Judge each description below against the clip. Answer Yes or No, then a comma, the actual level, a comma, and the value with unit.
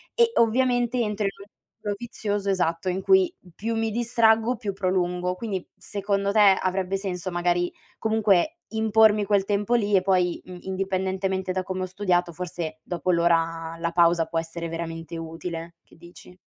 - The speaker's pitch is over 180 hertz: Yes, high, 190 Hz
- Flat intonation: No, average, 3.4 semitones